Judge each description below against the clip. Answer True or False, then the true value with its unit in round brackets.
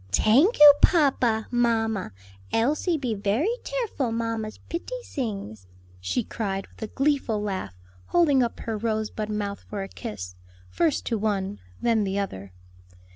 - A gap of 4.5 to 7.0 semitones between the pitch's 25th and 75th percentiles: True (5.2 semitones)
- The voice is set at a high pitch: True (220 Hz)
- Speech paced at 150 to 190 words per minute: False (140 wpm)